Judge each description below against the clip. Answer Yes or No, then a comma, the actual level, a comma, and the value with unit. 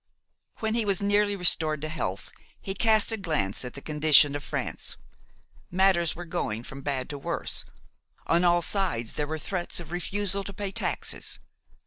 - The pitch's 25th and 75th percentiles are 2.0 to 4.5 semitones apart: No, average, 5.2 semitones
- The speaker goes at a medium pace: Yes, average, 170 wpm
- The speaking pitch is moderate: Yes, medium, 175 Hz